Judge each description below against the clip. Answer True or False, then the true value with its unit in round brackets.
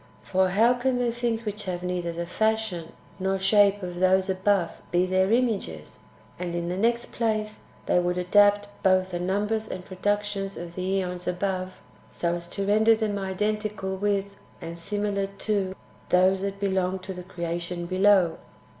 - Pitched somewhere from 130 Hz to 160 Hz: False (190 Hz)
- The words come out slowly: False (170 wpm)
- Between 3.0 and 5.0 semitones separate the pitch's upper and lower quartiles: False (2.4 semitones)